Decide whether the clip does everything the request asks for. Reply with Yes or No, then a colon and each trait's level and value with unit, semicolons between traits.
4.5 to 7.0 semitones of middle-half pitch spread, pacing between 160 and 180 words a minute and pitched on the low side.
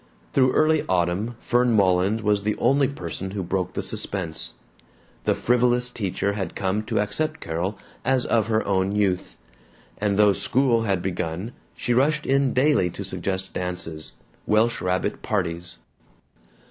No: average, 4.9 semitones; average, 145 wpm; low, 100 Hz